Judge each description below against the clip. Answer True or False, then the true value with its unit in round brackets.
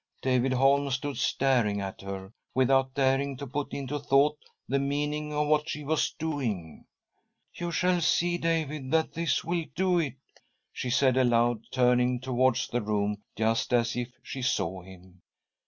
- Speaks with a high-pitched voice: False (130 Hz)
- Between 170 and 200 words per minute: False (155 wpm)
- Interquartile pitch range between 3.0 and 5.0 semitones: True (3.7 semitones)